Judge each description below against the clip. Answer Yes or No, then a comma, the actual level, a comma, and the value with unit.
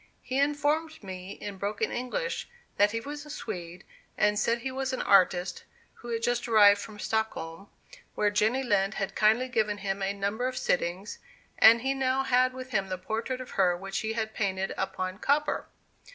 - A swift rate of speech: No, average, 185 wpm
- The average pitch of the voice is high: Yes, high, 220 Hz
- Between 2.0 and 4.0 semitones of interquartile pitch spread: No, average, 4.7 semitones